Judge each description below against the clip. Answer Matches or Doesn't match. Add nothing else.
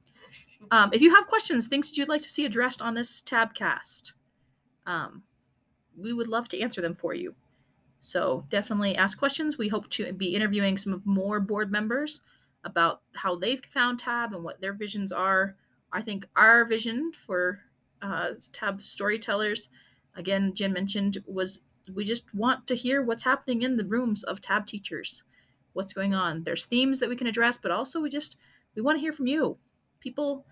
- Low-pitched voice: Doesn't match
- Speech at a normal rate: Matches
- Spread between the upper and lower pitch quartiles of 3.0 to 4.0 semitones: Doesn't match